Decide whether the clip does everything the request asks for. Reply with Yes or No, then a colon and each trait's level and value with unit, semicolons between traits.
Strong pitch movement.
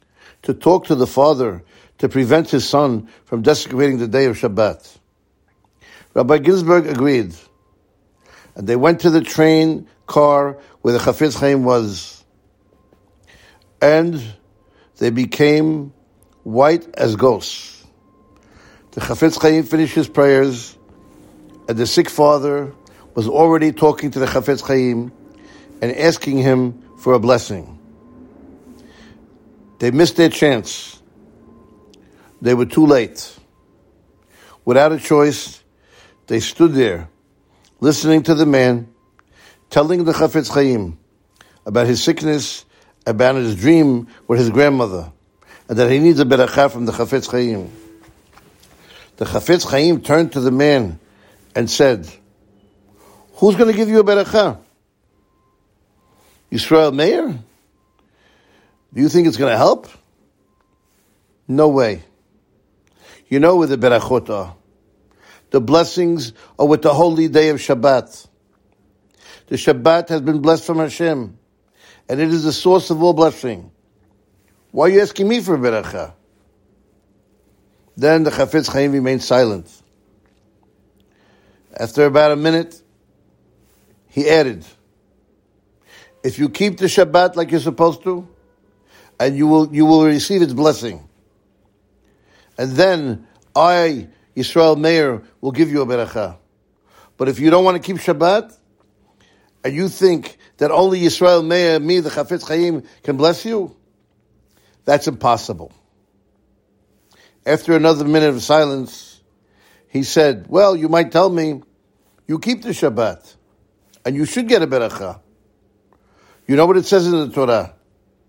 Yes: wide, 7.2 semitones